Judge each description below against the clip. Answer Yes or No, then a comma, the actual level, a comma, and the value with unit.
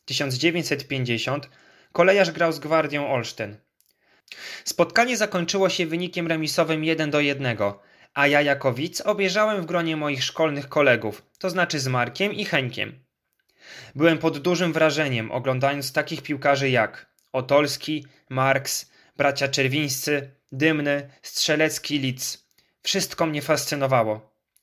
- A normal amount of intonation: Yes, average, 3.7 semitones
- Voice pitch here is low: No, medium, 145 Hz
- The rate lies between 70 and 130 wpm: Yes, average, 115 wpm